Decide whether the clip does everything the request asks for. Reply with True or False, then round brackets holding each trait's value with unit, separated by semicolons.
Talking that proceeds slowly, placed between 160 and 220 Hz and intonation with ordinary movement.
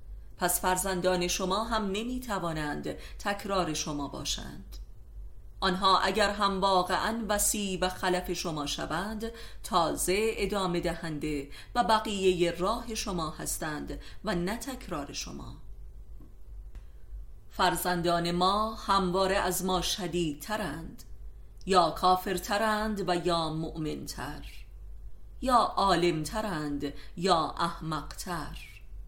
True (95 wpm; 185 Hz; 3.1 semitones)